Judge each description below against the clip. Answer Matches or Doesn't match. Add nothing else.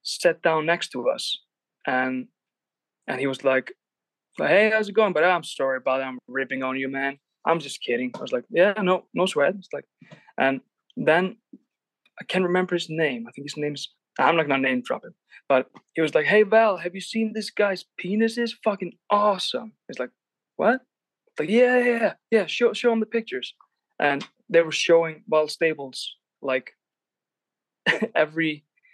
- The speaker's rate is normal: Matches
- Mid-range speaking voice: Matches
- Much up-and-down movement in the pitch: Matches